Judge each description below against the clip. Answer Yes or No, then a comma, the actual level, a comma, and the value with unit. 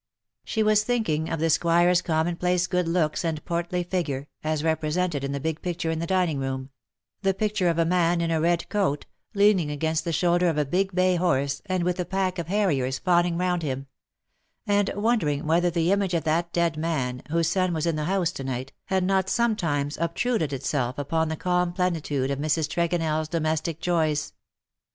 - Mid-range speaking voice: Yes, medium, 170 Hz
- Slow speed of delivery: No, average, 195 wpm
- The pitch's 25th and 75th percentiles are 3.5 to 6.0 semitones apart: No, average, 2.8 semitones